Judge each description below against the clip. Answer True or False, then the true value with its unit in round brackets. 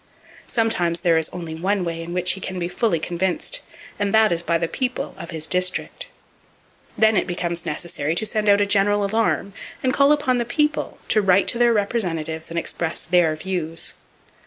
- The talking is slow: False (190 wpm)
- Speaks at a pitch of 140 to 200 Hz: True (185 Hz)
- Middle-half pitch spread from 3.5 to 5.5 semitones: True (4.4 semitones)